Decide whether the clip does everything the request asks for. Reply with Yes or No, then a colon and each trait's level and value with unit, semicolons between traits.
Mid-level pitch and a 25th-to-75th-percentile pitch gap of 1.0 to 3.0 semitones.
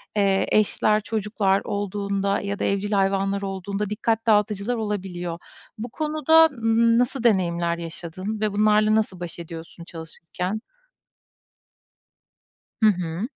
No: high, 200 Hz; average, 2.7 semitones